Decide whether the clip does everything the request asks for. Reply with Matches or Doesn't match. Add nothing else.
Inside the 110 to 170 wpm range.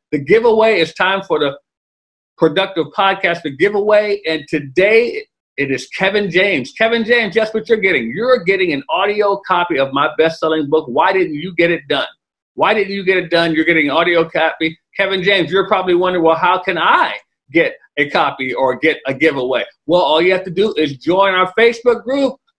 Doesn't match